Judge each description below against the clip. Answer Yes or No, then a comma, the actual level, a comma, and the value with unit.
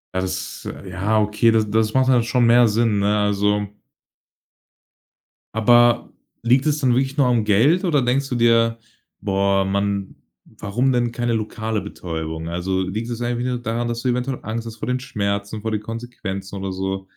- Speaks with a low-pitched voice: Yes, low, 110 Hz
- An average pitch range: Yes, average, 3.3 semitones